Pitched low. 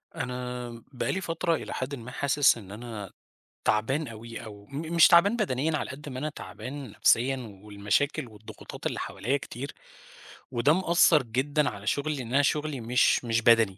Yes: low, 130 Hz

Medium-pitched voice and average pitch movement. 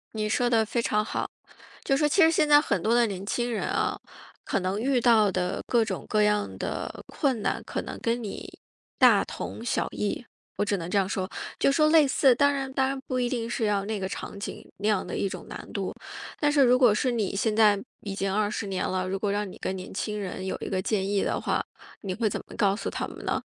No: high, 215 Hz; average, 3.8 semitones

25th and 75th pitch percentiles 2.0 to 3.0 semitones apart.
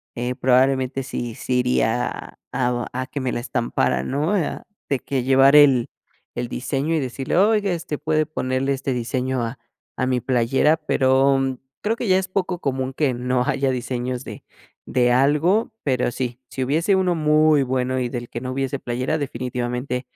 Yes: average, 2.7 semitones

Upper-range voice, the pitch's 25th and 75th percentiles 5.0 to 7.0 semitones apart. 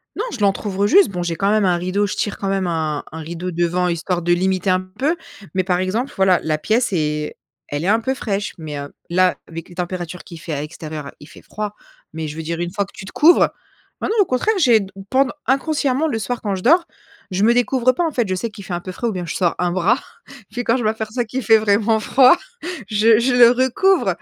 Yes: high, 195 Hz; average, 5.3 semitones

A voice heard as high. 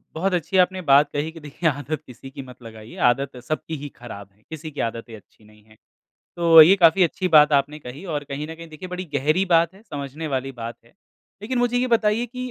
No: medium, 150 Hz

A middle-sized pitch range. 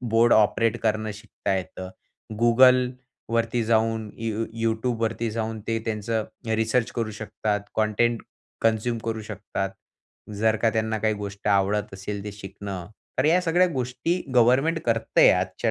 No: narrow, 1.9 semitones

